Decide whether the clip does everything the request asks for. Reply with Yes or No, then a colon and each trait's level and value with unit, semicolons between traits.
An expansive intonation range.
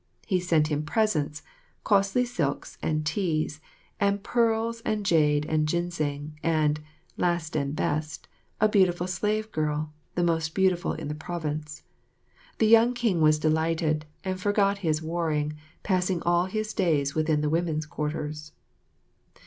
No: average, 4.1 semitones